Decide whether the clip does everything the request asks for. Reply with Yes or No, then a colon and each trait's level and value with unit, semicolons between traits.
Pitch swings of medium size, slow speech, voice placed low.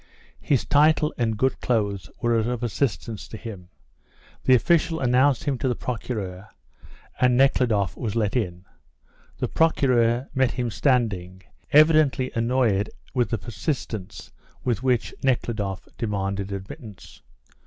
Yes: average, 4.2 semitones; slow, 125 wpm; low, 120 Hz